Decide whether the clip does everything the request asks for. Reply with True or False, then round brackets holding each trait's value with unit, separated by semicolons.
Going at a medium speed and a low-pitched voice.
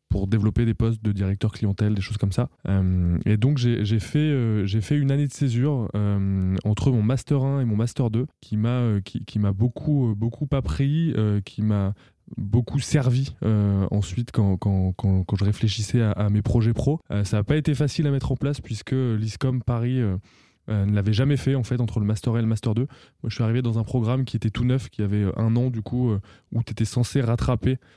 False (235 wpm; 115 Hz)